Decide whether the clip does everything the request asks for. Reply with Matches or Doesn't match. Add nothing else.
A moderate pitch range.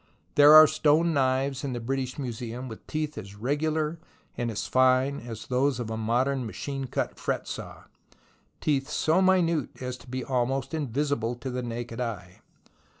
Matches